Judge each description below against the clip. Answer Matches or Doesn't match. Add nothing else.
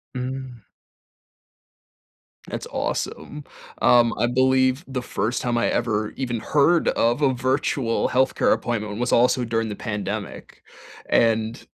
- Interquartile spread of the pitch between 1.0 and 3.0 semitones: Matches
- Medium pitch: Doesn't match